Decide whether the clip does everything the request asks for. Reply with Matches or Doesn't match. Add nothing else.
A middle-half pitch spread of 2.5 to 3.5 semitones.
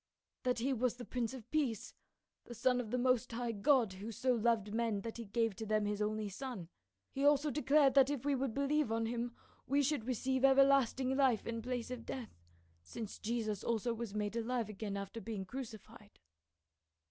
Matches